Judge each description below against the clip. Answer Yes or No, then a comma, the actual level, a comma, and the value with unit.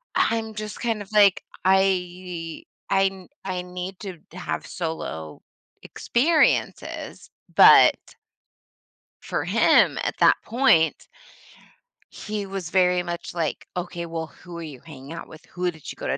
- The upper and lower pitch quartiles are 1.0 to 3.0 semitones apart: Yes, average, 2.7 semitones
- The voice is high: No, medium, 180 Hz